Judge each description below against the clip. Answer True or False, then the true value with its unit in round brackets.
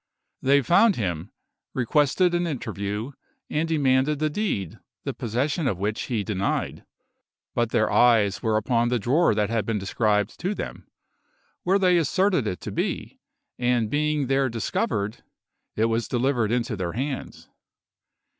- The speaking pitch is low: True (120 Hz)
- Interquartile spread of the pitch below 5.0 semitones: False (5.6 semitones)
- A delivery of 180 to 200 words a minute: False (145 wpm)